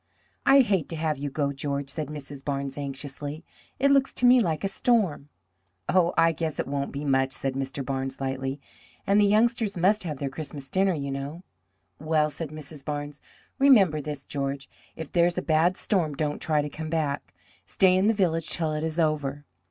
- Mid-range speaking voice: Yes, medium, 150 Hz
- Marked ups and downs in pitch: No, average, 3.8 semitones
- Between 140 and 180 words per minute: No, average, 200 wpm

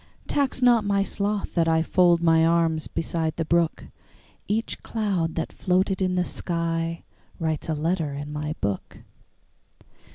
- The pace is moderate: No, slow, 130 wpm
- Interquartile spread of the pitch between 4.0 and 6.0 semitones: No, average, 2.8 semitones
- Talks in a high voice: No, medium, 170 Hz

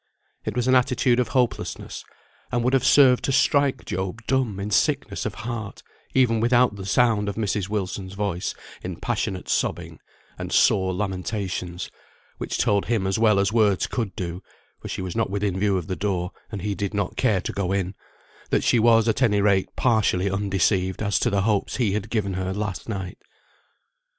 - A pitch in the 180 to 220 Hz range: No, low, 100 Hz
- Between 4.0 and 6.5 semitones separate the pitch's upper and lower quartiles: No, average, 3.2 semitones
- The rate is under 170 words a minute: No, average, 190 wpm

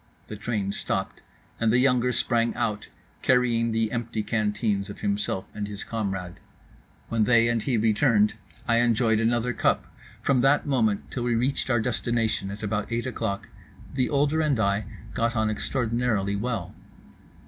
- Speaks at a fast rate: No, average, 160 wpm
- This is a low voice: Yes, low, 115 Hz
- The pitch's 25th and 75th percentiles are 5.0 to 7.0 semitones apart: No, average, 2.7 semitones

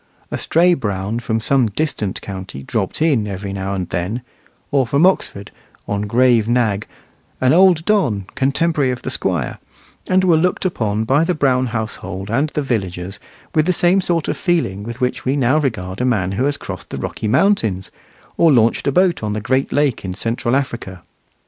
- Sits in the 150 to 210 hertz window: No, low, 120 Hz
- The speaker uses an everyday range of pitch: No, wide, 6.8 semitones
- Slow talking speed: No, average, 185 wpm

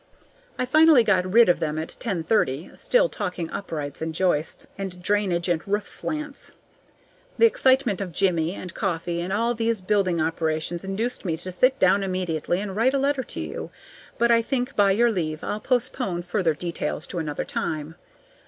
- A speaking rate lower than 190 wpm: Yes, average, 180 wpm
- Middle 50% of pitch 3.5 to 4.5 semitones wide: No, average, 5.3 semitones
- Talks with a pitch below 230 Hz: Yes, high, 190 Hz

